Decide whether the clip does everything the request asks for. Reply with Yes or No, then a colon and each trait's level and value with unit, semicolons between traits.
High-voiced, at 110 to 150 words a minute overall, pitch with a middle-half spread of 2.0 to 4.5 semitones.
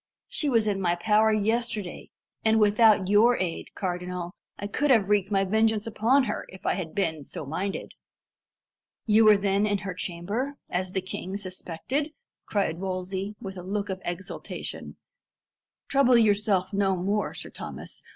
No: high, 200 Hz; average, 160 wpm; average, 2.8 semitones